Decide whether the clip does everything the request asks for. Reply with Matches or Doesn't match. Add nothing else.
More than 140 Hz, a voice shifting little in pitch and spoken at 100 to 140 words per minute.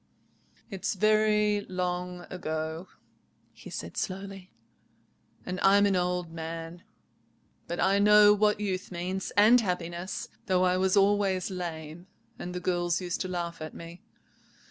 Matches